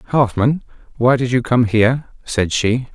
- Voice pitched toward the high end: No, low, 120 Hz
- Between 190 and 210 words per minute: No, average, 165 wpm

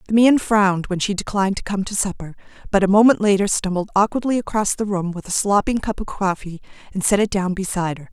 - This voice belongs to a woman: Yes, female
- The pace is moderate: No, fast, 230 wpm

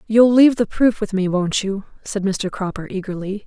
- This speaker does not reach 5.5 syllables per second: Yes, 5.1 syllables/s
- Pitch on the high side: Yes, high, 205 Hz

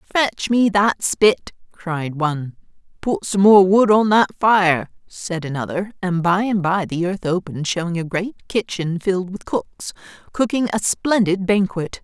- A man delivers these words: No, female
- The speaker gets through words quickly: No, average, 165 wpm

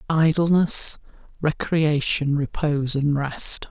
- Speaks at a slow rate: Yes, slow, 80 wpm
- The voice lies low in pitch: No, medium, 150 Hz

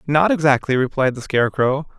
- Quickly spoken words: No, average, 150 wpm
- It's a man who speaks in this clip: Yes, male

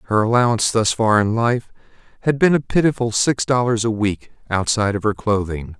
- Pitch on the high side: No, low, 110 Hz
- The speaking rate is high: No, average, 185 wpm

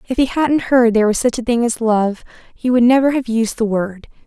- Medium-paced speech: No, fast, 255 wpm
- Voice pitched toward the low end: No, high, 235 Hz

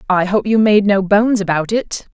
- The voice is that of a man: No, female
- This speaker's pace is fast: Yes, fast, 225 wpm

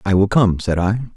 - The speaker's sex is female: No, male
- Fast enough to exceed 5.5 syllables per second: No, 5.3 syllables/s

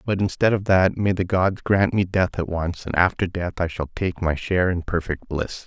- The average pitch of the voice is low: Yes, very low, 90 Hz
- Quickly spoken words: Yes, fast, 245 wpm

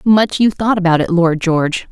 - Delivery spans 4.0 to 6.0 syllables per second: Yes, 5.0 syllables/s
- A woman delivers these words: Yes, female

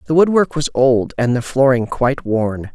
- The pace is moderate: Yes, average, 195 wpm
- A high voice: No, low, 130 Hz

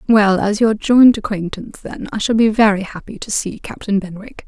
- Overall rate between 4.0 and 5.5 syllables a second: Yes, 5.2 syllables/s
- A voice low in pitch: No, high, 210 Hz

